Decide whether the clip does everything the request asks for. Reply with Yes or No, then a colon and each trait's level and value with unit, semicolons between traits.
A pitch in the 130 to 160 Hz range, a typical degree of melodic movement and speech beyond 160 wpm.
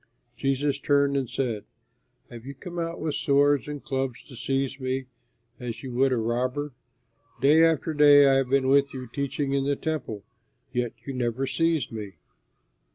No: low, 135 Hz; narrow, 2.1 semitones; average, 170 wpm